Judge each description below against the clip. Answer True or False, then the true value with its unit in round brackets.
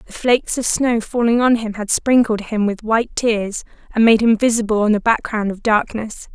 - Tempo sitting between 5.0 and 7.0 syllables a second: True (5.1 syllables/s)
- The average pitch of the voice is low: False (220 Hz)